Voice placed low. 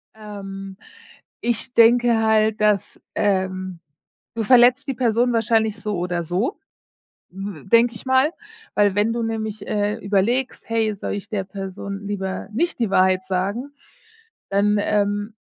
No: high, 210 Hz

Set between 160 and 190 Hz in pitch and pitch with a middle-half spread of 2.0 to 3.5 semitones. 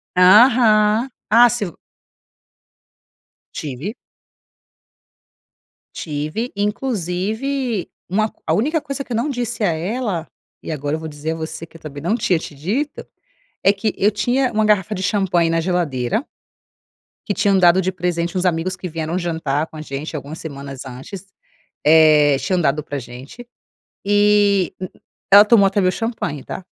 No: medium, 185 Hz; average, 5.2 semitones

